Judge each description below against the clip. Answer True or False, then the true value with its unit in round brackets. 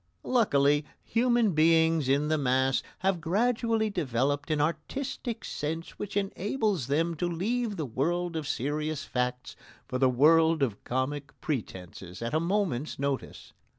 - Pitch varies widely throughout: True (5.7 semitones)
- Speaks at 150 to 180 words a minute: False (140 wpm)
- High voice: False (155 Hz)